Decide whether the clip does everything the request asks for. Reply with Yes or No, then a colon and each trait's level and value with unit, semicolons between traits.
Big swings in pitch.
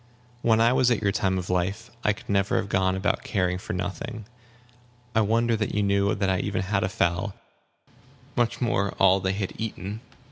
No: narrow, 2.6 semitones